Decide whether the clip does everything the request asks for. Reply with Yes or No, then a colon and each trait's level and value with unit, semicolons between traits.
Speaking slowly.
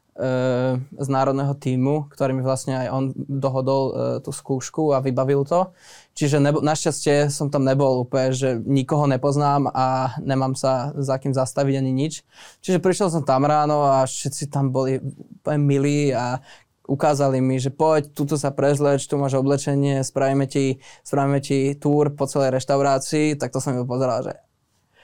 No: average, 160 wpm